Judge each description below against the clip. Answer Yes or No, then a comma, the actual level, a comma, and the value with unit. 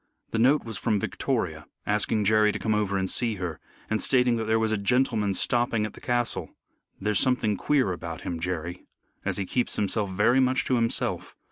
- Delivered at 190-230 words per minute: Yes, average, 200 wpm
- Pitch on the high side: No, low, 110 Hz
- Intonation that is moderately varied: Yes, average, 3.4 semitones